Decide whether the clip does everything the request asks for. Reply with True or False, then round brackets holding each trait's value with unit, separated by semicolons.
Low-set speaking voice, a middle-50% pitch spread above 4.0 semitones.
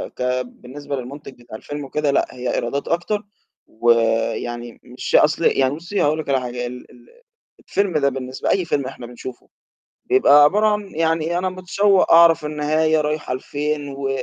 False (145 Hz; 4.5 semitones)